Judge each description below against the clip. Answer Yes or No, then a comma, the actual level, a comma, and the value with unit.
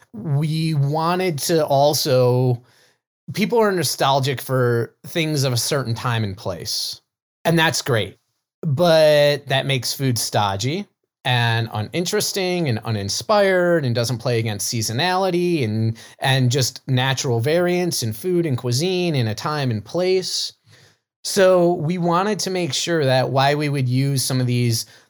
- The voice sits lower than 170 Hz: Yes, low, 135 Hz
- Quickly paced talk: No, average, 145 wpm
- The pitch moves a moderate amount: No, wide, 6.0 semitones